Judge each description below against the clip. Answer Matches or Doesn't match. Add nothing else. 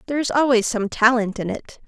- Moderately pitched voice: Doesn't match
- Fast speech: Matches